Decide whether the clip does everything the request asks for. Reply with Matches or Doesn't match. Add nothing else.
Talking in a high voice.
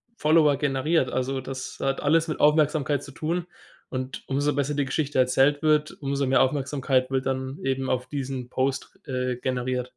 Doesn't match